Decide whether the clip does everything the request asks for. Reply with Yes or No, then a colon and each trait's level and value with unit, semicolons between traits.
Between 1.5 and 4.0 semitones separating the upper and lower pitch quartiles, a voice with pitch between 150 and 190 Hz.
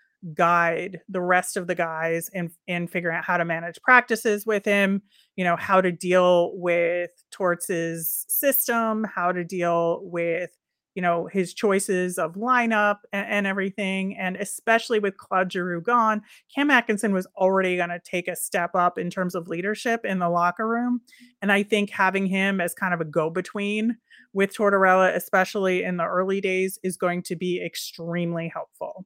Yes: average, 2.8 semitones; medium, 185 Hz